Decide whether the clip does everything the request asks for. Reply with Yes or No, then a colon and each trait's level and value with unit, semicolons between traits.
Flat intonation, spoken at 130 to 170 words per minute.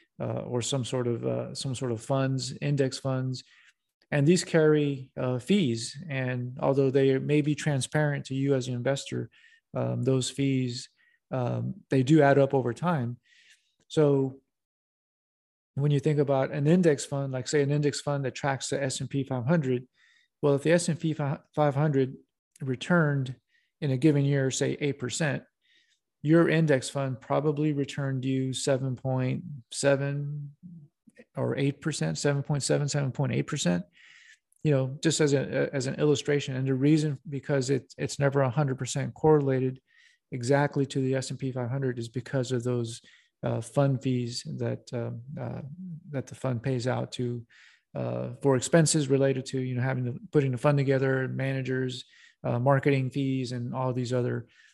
Yes: narrow, 2.1 semitones; average, 160 wpm